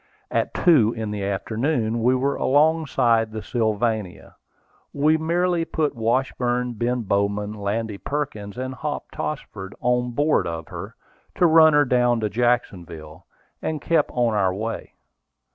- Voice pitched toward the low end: Yes, low, 120 Hz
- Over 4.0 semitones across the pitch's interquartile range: Yes, wide, 5.4 semitones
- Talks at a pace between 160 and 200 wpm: No, average, 140 wpm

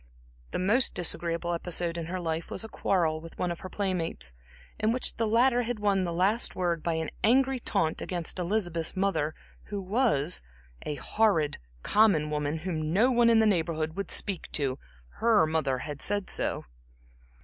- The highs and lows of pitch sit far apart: No, average, 4.8 semitones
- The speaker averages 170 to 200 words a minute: Yes, average, 175 wpm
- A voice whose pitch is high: No, medium, 180 Hz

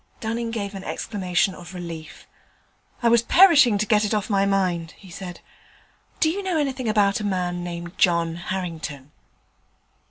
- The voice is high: Yes, high, 195 Hz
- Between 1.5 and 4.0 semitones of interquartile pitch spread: No, average, 4.4 semitones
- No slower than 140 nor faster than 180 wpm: Yes, average, 160 wpm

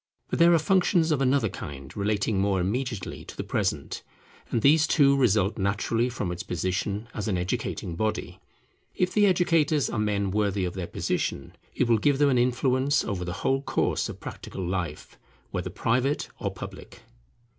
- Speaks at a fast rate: No, average, 175 wpm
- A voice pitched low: Yes, low, 110 Hz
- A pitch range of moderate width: No, wide, 6.2 semitones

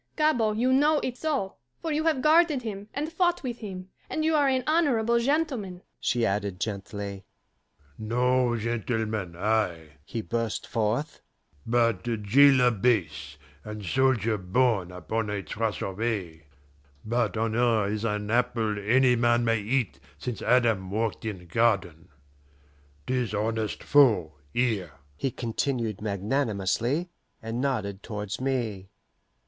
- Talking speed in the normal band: No, slow, 130 wpm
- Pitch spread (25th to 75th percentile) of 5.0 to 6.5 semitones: Yes, wide, 5.6 semitones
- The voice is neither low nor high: No, low, 115 Hz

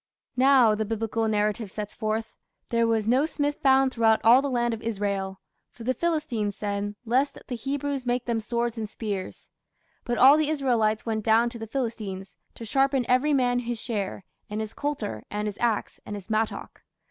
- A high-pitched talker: Yes, high, 230 Hz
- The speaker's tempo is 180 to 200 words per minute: Yes, average, 185 wpm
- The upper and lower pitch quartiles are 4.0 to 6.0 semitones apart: No, average, 3.2 semitones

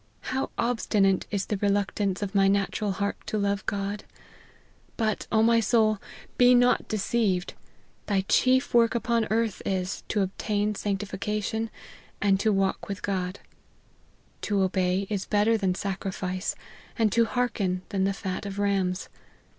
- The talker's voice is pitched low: No, high, 200 Hz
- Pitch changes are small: Yes, narrow, 2.3 semitones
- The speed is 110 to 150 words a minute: Yes, average, 145 wpm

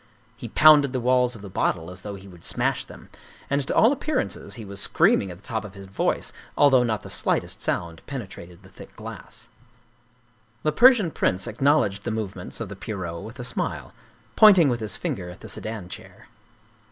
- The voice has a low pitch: Yes, low, 110 Hz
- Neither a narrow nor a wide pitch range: No, wide, 5.8 semitones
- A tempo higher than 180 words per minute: Yes, average, 200 wpm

